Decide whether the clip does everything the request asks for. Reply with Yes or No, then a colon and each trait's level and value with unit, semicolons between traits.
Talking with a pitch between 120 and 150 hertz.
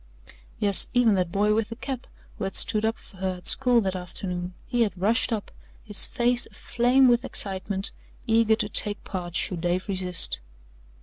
No: high, 205 Hz